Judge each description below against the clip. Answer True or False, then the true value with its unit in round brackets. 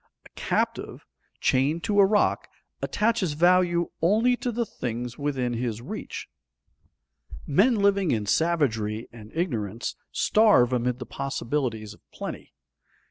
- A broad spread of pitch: True (8.7 semitones)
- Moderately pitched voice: True (145 Hz)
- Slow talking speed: True (125 wpm)